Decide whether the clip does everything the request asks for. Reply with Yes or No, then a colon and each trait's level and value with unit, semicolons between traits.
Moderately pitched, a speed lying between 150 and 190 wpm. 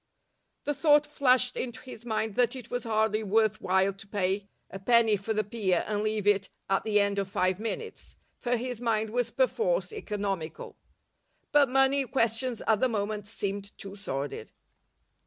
No: high, 220 Hz; average, 170 wpm